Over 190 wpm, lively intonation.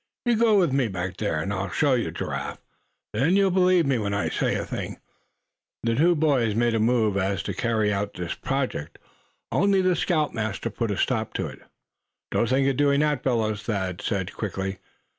Yes: average, 200 wpm; wide, 6.3 semitones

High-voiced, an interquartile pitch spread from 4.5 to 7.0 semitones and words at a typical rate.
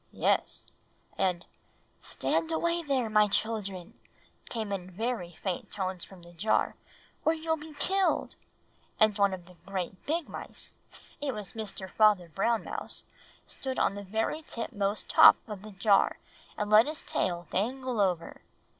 Yes: high, 210 Hz; average, 5.0 semitones; average, 155 wpm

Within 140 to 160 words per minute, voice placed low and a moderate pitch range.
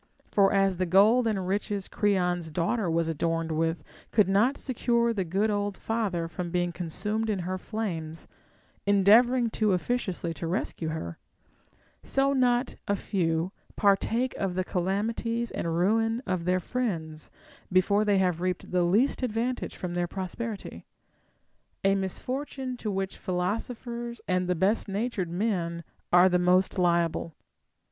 No: average, 145 wpm; high, 195 Hz; average, 4.2 semitones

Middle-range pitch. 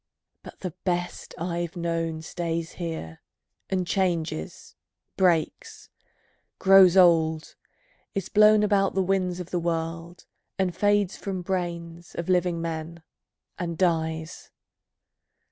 Yes: medium, 175 Hz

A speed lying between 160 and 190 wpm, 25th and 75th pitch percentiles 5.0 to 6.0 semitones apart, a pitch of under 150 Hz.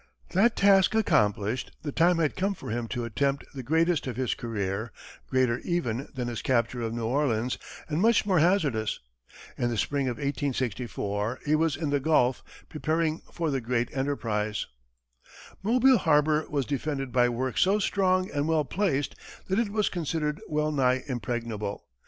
Yes: average, 165 wpm; average, 5.3 semitones; medium, 140 Hz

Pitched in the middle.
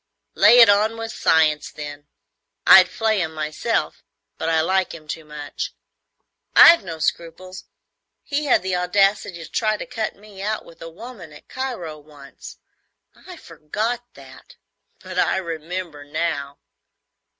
Yes: medium, 180 Hz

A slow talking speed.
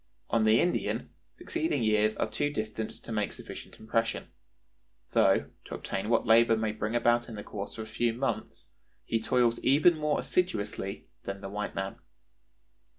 No: average, 165 wpm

